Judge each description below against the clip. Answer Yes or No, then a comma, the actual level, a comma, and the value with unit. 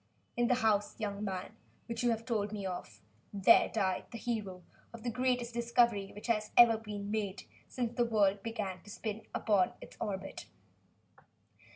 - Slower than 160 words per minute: No, average, 170 wpm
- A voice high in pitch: Yes, high, 215 Hz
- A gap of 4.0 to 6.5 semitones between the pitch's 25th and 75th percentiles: No, average, 2.7 semitones